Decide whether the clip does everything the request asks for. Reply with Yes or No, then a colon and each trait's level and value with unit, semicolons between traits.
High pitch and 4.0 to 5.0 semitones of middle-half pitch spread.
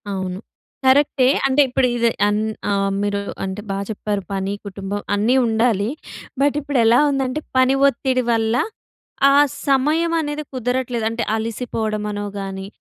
Yes: high, 230 Hz; average, 4.3 semitones